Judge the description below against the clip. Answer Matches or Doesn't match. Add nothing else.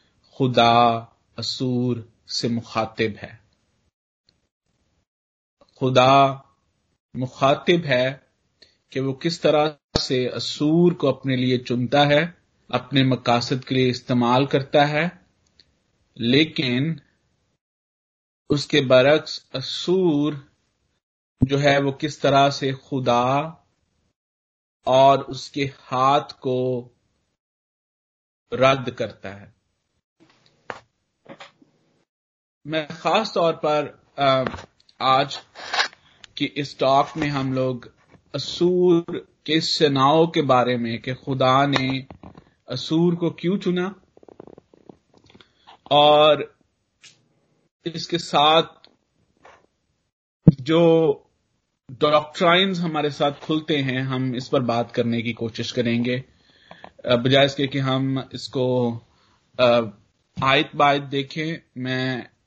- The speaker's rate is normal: Doesn't match